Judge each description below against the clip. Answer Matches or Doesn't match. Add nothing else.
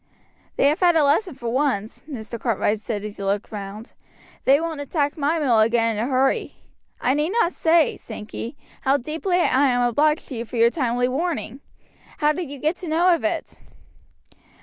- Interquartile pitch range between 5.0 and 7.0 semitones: Matches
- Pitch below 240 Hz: Doesn't match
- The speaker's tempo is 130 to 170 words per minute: Doesn't match